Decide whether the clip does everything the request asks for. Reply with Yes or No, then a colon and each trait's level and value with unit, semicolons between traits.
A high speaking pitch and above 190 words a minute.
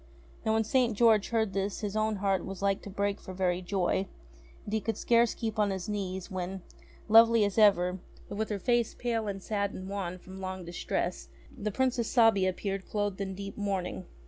Yes: high, 200 Hz; average, 200 wpm